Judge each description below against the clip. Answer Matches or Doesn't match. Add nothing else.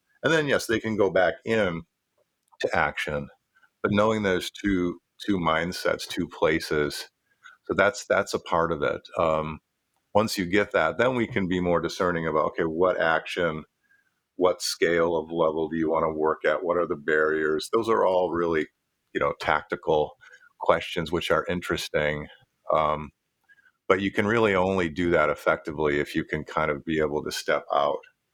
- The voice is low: Matches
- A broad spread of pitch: Matches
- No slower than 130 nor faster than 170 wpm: Doesn't match